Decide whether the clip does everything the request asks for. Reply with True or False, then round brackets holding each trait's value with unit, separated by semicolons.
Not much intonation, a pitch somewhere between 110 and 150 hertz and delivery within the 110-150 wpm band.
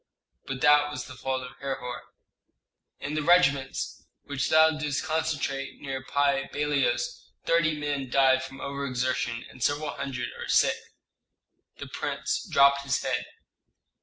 True (1.8 semitones; 140 Hz; 140 wpm)